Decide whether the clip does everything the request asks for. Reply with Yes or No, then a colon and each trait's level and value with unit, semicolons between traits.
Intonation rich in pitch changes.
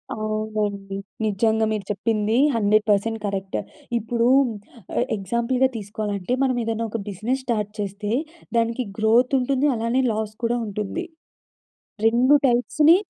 No: narrow, 2.4 semitones